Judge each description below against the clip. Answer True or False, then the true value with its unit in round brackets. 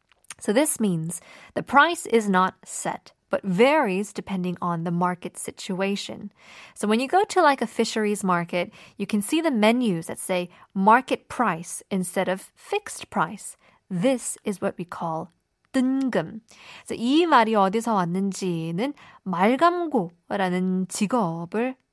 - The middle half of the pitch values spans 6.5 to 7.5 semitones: False (5.3 semitones)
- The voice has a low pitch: False (205 Hz)